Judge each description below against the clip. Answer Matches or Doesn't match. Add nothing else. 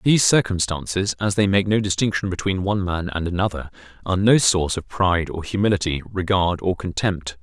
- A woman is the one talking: Doesn't match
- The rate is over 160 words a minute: Matches